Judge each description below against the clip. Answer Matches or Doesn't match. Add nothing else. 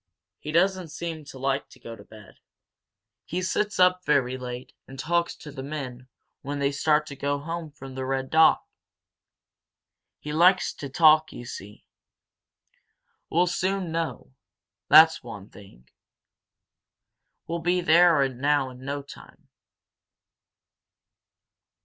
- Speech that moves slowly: Matches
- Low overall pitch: Doesn't match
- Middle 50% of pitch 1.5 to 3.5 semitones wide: Doesn't match